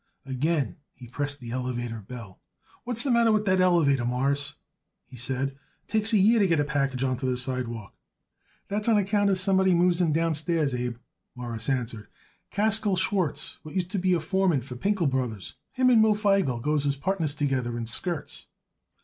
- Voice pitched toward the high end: No, medium, 150 Hz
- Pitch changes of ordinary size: No, wide, 7.1 semitones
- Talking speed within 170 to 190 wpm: Yes, average, 185 wpm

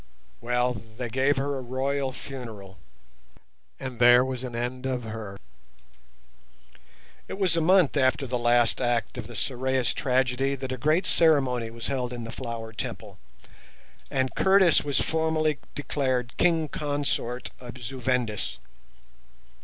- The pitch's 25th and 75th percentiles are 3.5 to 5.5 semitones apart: No, average, 2.7 semitones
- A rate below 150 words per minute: Yes, average, 140 wpm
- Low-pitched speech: Yes, low, 130 Hz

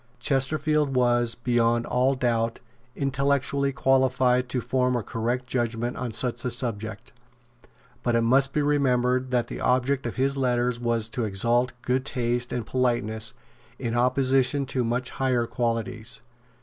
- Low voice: Yes, low, 125 Hz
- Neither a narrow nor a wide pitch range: No, narrow, 1.8 semitones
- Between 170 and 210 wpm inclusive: No, average, 145 wpm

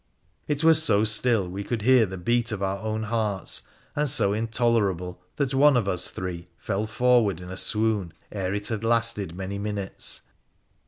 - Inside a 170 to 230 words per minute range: Yes, average, 175 wpm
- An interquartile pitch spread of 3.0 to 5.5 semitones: Yes, average, 3.5 semitones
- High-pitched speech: No, low, 105 Hz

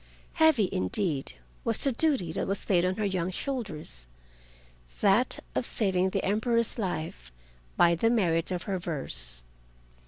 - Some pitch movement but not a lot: No, wide, 8.5 semitones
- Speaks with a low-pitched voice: No, medium, 180 Hz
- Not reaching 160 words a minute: Yes, slow, 135 wpm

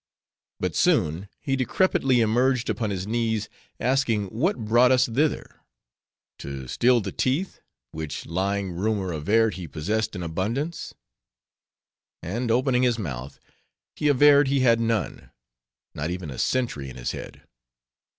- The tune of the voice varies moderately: No, wide, 6.0 semitones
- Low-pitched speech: Yes, low, 110 Hz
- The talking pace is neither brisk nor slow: No, slow, 130 wpm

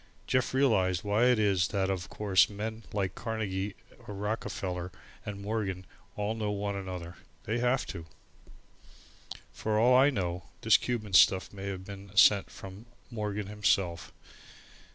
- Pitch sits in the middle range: No, low, 100 Hz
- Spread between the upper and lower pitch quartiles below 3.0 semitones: Yes, narrow, 2.4 semitones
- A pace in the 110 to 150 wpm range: Yes, average, 145 wpm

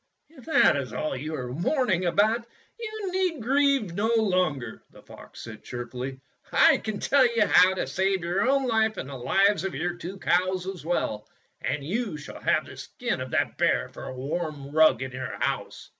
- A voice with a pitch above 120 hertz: Yes, medium, 185 Hz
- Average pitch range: No, wide, 7.7 semitones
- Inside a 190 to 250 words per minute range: Yes, average, 195 wpm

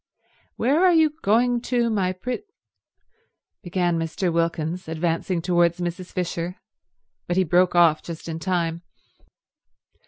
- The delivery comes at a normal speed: No, slow, 125 wpm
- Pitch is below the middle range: No, medium, 180 Hz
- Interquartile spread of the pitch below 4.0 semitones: Yes, average, 3.6 semitones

